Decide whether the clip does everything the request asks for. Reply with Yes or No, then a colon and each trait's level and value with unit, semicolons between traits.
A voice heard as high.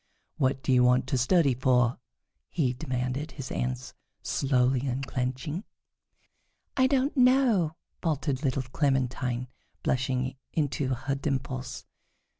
No: low, 130 Hz